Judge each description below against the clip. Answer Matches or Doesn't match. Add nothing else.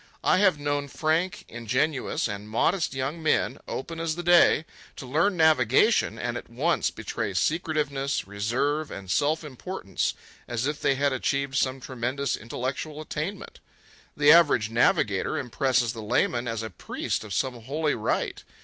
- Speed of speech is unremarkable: Matches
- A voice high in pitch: Doesn't match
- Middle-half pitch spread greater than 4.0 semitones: Matches